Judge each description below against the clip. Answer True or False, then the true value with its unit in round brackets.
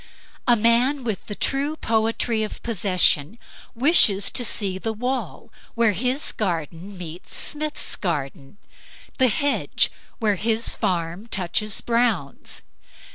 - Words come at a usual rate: False (120 wpm)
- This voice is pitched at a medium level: False (220 Hz)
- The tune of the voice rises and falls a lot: False (4.6 semitones)